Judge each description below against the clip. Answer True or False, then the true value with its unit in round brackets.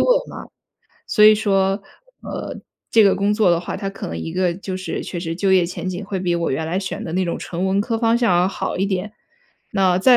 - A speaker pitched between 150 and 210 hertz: True (190 Hz)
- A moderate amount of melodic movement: False (2.3 semitones)